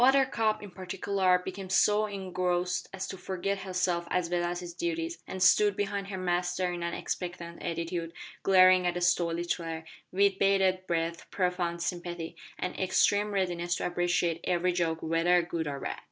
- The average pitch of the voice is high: No, medium, 180 Hz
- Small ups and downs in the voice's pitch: Yes, narrow, 1.8 semitones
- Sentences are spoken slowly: No, average, 170 wpm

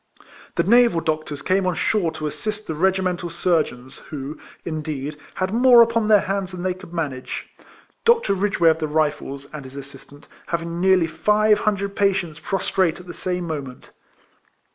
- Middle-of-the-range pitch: Yes, medium, 175 Hz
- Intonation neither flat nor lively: Yes, average, 4.2 semitones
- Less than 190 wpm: Yes, average, 165 wpm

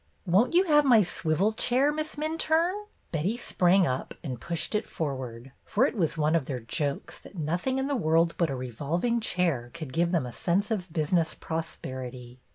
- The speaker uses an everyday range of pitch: No, wide, 8.1 semitones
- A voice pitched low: No, medium, 170 Hz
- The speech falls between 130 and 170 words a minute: No, average, 185 wpm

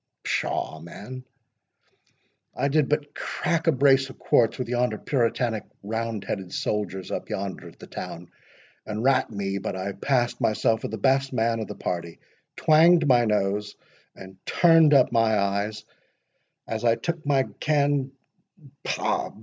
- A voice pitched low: Yes, low, 115 Hz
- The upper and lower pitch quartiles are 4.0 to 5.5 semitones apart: Yes, average, 5.1 semitones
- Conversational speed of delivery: Yes, average, 145 wpm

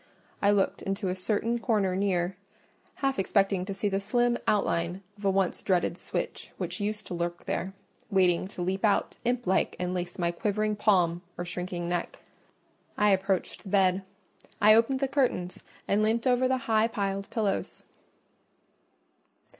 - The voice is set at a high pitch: Yes, high, 195 Hz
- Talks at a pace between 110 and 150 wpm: No, average, 160 wpm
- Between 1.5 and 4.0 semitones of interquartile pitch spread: Yes, average, 2.9 semitones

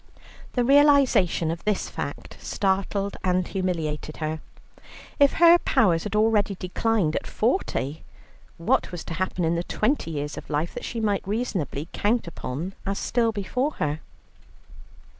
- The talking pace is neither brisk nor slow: Yes, average, 145 wpm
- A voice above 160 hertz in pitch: Yes, high, 190 Hz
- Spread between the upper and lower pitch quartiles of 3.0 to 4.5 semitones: No, wide, 5.5 semitones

